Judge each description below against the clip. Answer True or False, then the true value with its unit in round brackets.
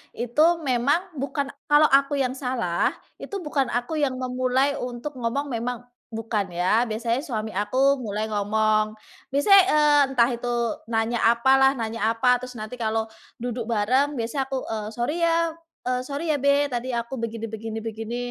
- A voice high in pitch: True (245 Hz)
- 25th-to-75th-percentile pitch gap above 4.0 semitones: False (3.4 semitones)